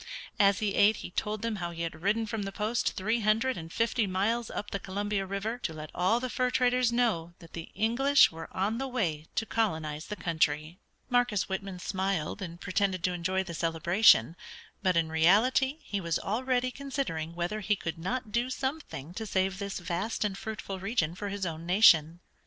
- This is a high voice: Yes, high, 195 Hz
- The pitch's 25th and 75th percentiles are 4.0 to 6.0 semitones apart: Yes, average, 4.8 semitones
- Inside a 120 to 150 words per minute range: No, average, 195 wpm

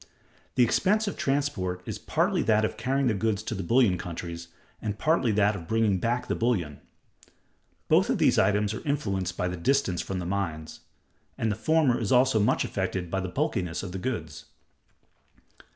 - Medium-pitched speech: No, low, 105 Hz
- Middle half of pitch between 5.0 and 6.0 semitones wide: Yes, wide, 5.4 semitones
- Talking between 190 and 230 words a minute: No, average, 180 wpm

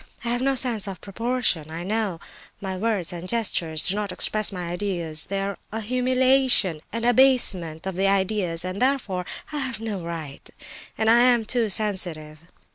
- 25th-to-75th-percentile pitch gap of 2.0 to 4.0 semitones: No, average, 4.9 semitones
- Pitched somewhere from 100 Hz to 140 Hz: No, high, 200 Hz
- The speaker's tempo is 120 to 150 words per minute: No, average, 165 wpm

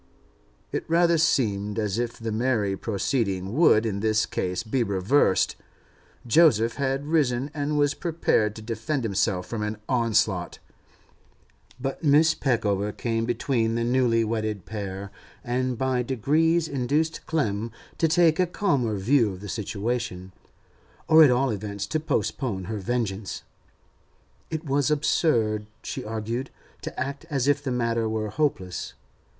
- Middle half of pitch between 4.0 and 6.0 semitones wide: Yes, average, 5.0 semitones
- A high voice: No, low, 115 Hz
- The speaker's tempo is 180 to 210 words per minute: No, average, 140 wpm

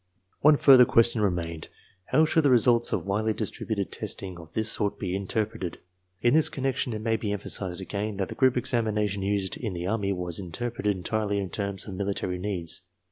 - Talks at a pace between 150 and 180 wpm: No, average, 195 wpm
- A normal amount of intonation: Yes, average, 3.4 semitones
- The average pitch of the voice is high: No, low, 105 Hz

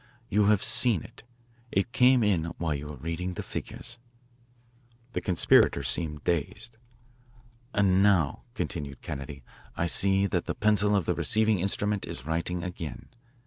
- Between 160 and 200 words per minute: No, average, 145 wpm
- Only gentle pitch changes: No, average, 4.8 semitones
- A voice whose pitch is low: Yes, very low, 90 Hz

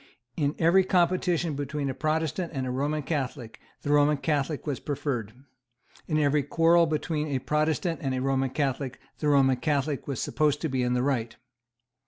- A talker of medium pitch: Yes, medium, 145 Hz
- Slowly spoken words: No, average, 175 wpm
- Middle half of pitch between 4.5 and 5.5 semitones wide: No, narrow, 2.6 semitones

